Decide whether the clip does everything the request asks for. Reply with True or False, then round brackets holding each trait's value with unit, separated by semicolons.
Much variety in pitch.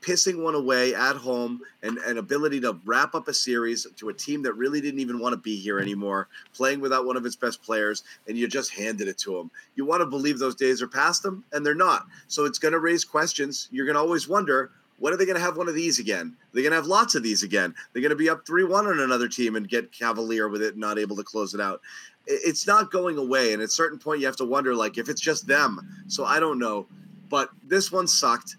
True (6.9 semitones)